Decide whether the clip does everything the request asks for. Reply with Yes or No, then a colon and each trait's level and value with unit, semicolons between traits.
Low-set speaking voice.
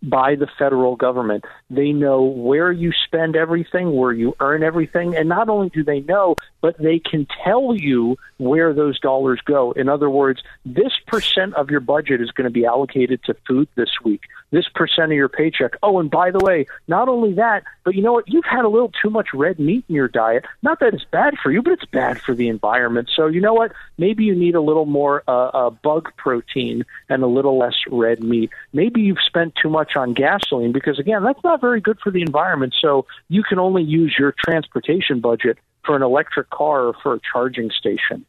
No: medium, 150 Hz